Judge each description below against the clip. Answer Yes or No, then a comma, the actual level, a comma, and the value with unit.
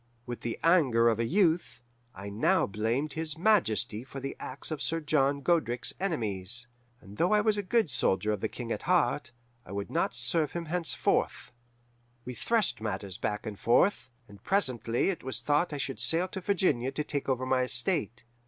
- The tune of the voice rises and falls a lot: Yes, wide, 6.4 semitones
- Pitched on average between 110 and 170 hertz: Yes, low, 135 Hz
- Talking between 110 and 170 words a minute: No, average, 190 wpm